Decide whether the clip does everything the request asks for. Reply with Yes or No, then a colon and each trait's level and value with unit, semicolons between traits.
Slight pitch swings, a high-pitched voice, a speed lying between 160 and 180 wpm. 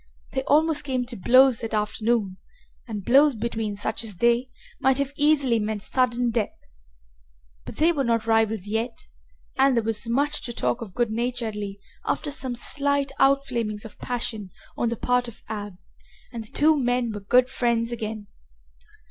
No: average, 3.2 semitones; high, 235 Hz; average, 165 wpm